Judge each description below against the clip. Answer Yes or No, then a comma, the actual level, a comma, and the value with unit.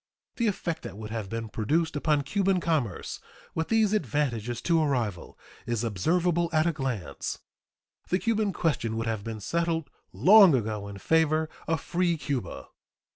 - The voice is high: No, medium, 150 Hz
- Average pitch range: No, wide, 7.1 semitones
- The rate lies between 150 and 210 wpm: Yes, average, 160 wpm